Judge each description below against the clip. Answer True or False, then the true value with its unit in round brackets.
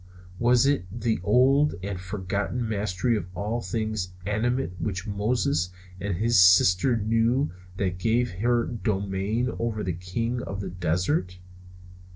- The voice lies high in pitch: False (105 Hz)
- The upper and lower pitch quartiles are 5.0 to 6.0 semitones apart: False (4.1 semitones)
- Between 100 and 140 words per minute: True (135 wpm)